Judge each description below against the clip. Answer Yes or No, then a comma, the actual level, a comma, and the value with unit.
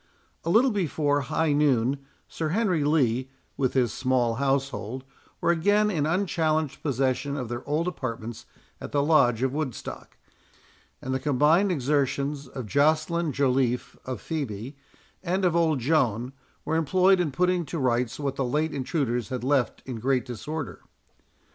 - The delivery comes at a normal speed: Yes, average, 150 wpm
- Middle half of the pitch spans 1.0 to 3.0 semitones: No, average, 3.9 semitones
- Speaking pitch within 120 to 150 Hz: Yes, medium, 140 Hz